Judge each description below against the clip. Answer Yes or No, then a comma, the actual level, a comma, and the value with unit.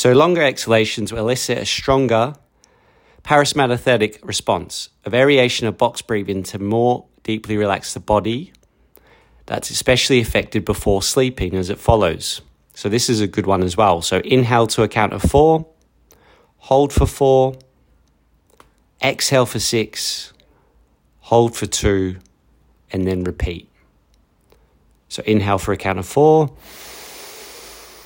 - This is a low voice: Yes, low, 110 Hz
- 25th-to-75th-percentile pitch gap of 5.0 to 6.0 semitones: Yes, wide, 5.6 semitones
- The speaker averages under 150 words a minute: Yes, slow, 135 wpm